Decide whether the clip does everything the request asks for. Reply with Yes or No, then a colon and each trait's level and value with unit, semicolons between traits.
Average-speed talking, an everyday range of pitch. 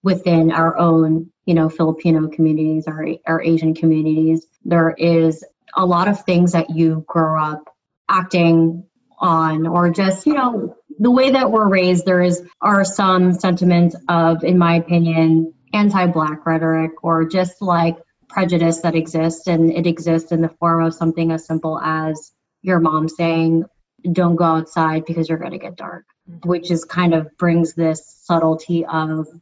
No: average, 165 wpm; narrow, 1.7 semitones